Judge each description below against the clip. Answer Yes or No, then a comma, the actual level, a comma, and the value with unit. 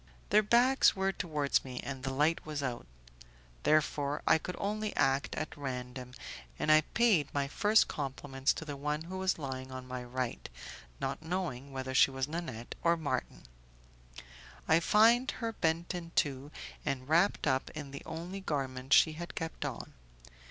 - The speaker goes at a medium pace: Yes, average, 165 wpm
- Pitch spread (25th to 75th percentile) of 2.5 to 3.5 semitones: No, average, 4.5 semitones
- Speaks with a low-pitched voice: No, medium, 150 Hz